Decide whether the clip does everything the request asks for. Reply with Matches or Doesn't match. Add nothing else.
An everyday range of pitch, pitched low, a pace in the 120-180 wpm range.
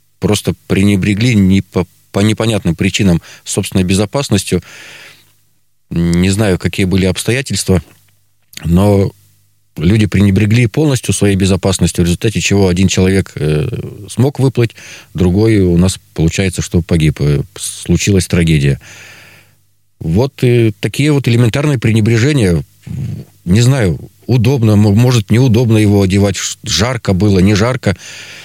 Doesn't match